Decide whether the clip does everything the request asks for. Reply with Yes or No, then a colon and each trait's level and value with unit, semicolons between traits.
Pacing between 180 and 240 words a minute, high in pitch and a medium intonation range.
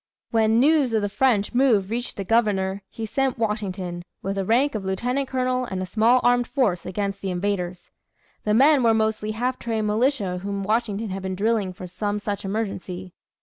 Yes: average, 190 wpm; high, 215 Hz; average, 3.7 semitones